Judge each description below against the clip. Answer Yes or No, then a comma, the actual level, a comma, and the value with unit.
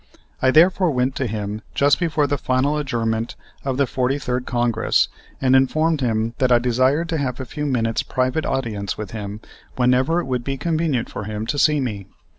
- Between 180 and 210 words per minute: Yes, average, 190 wpm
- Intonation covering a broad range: No, average, 3.7 semitones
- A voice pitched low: Yes, low, 130 Hz